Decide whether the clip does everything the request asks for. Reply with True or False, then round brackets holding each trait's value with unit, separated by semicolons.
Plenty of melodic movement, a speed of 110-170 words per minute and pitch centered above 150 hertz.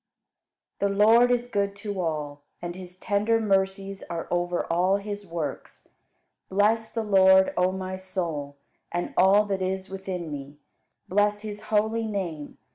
False (2.7 semitones; 150 wpm; 190 Hz)